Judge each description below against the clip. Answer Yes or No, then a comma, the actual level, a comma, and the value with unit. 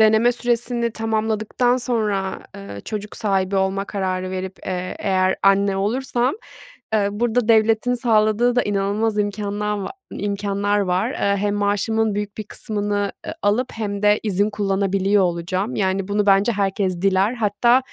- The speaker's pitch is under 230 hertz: Yes, high, 205 Hz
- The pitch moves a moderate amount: No, narrow, 2.2 semitones